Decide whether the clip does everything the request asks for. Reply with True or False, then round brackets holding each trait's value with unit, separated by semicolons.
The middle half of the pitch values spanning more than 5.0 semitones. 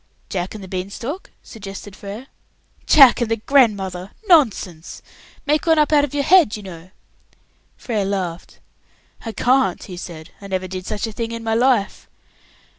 True (5.4 semitones)